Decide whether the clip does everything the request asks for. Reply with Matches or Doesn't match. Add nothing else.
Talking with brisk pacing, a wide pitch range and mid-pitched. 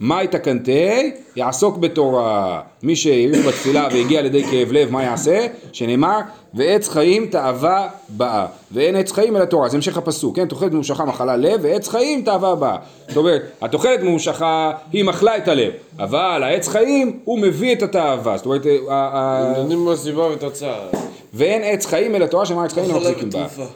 Matches